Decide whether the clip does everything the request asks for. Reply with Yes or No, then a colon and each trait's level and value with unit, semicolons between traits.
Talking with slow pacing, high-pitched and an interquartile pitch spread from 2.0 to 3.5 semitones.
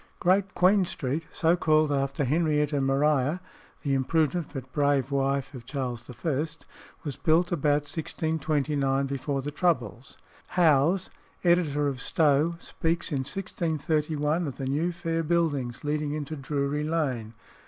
No: slow, 130 wpm; medium, 150 Hz; average, 3.1 semitones